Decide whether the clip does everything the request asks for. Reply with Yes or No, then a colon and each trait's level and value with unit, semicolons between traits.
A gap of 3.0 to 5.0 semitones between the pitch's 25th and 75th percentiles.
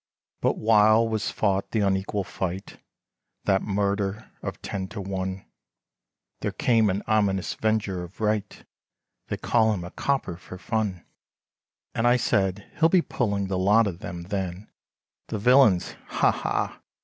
No: narrow, 2.5 semitones